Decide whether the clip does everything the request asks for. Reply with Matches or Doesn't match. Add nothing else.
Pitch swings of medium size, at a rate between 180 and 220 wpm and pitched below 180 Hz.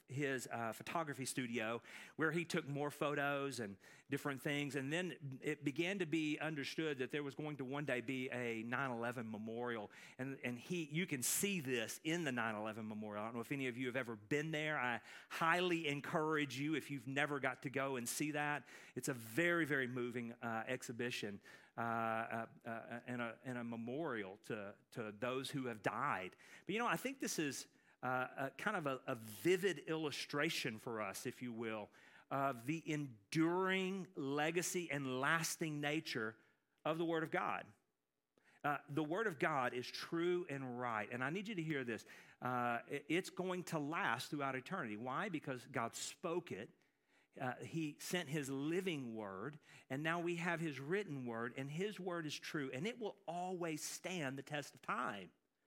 Matches